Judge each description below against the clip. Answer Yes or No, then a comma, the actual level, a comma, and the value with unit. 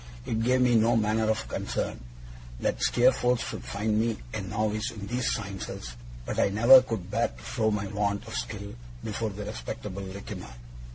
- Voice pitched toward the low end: Yes, low, 110 Hz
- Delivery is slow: No, average, 175 wpm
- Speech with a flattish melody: Yes, narrow, 2.3 semitones